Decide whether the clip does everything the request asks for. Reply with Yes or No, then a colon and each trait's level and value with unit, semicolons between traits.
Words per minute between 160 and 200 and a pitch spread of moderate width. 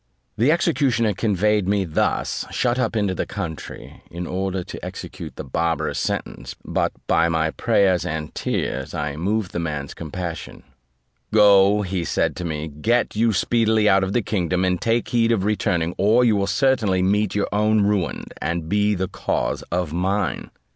Yes: average, 170 wpm; average, 3.9 semitones